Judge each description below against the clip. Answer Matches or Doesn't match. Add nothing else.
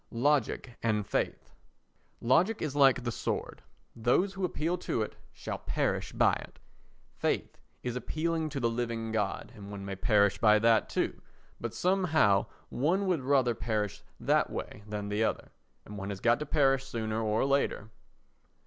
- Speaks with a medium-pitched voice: Doesn't match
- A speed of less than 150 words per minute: Doesn't match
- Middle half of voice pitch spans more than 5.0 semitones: Matches